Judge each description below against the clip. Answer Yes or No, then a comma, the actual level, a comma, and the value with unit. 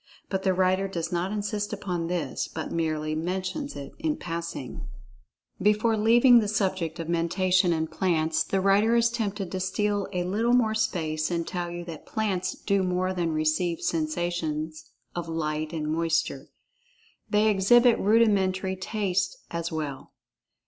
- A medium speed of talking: Yes, average, 155 wpm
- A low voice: No, medium, 185 Hz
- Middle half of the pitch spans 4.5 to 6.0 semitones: No, average, 3.8 semitones